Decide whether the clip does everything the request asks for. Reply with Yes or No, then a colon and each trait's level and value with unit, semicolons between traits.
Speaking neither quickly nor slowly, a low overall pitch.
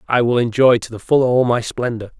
No: fast, 245 wpm; low, 120 Hz